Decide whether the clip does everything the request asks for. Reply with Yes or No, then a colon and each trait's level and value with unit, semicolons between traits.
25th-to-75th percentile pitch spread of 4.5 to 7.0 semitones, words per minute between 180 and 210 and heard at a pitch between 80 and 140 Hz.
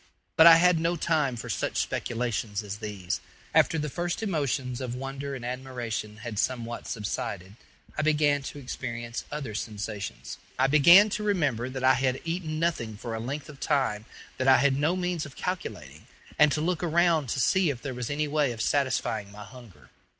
Yes: average, 5.0 semitones; average, 185 wpm; low, 135 Hz